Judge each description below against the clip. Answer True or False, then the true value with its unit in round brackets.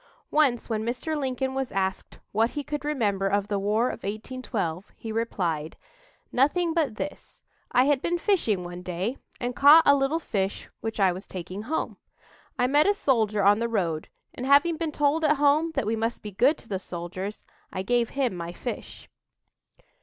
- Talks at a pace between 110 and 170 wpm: False (185 wpm)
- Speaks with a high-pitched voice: True (230 Hz)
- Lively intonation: True (6.4 semitones)